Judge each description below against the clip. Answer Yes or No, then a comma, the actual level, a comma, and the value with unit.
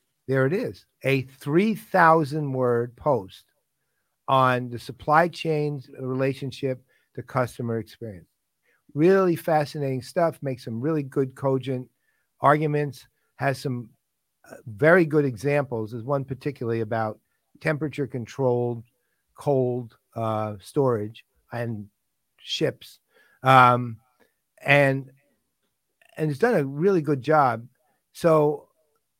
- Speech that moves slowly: Yes, slow, 95 wpm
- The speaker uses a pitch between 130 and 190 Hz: Yes, low, 135 Hz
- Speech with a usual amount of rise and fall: Yes, average, 3.3 semitones